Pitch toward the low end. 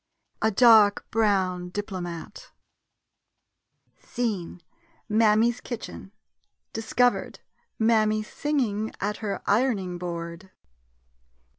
No: high, 210 Hz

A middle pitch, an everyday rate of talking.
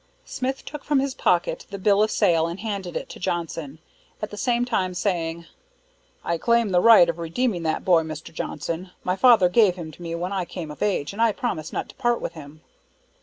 No: medium, 180 Hz; fast, 220 wpm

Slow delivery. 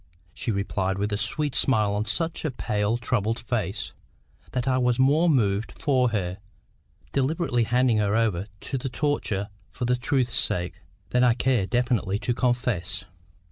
No: average, 160 wpm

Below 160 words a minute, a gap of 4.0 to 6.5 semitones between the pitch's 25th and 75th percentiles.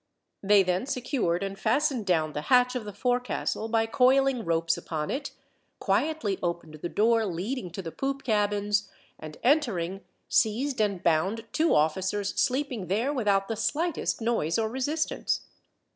Yes: average, 150 wpm; wide, 5.4 semitones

